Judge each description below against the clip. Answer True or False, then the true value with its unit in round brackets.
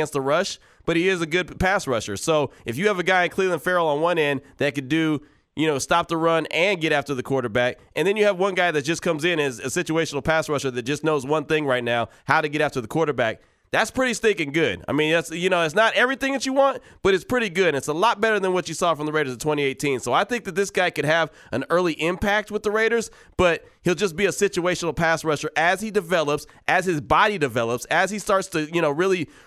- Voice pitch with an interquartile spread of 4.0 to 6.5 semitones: True (4.4 semitones)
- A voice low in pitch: False (165 Hz)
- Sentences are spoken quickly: True (265 wpm)